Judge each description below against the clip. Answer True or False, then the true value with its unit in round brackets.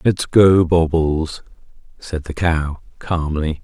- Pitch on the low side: True (80 Hz)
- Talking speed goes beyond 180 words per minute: False (100 wpm)